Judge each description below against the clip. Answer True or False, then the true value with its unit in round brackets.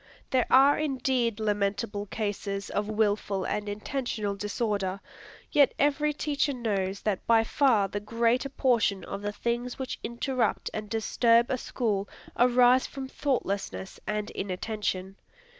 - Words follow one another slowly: True (130 wpm)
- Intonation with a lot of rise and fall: False (3.8 semitones)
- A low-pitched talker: False (225 Hz)